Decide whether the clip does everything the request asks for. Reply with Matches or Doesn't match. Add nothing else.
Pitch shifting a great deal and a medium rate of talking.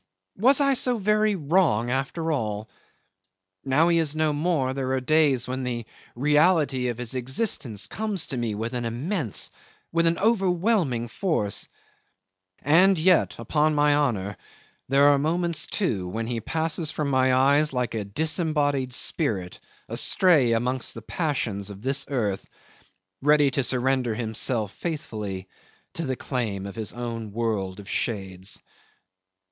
Matches